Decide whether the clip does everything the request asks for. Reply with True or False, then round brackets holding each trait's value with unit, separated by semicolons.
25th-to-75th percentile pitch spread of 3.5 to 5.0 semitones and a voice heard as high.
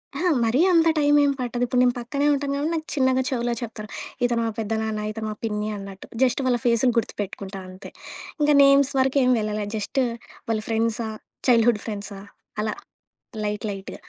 True (3.8 semitones; 235 Hz)